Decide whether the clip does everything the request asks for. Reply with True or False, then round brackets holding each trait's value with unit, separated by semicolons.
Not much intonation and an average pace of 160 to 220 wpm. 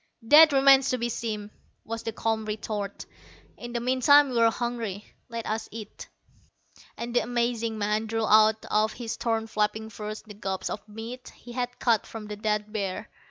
True (2.0 semitones; 175 wpm)